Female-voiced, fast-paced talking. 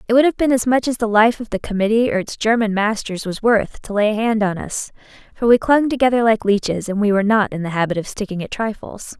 Yes: female; fast, 265 wpm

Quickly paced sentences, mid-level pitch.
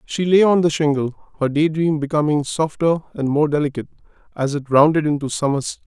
No: average, 190 wpm; medium, 150 Hz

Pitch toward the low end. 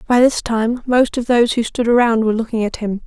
No: high, 230 Hz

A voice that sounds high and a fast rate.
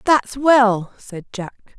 No: high, 230 Hz; slow, 135 wpm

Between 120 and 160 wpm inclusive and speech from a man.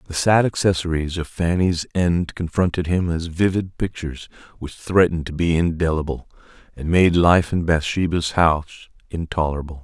Yes: average, 140 wpm; male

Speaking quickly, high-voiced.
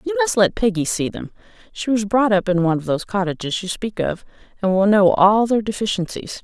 Yes: fast, 225 wpm; high, 195 Hz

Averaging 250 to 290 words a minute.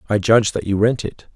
Yes: fast, 265 wpm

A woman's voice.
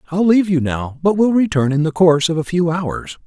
No: male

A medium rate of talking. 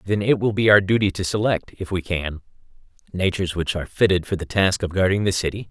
No: fast, 230 wpm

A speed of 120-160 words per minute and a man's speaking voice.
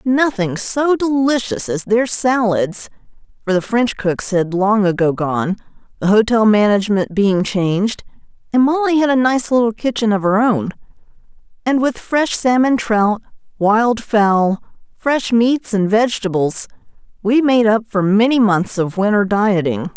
No: average, 145 wpm; female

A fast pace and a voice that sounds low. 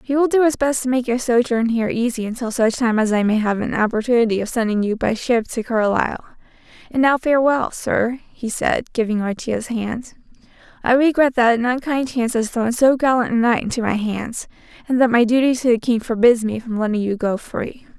No: fast, 220 wpm; high, 235 Hz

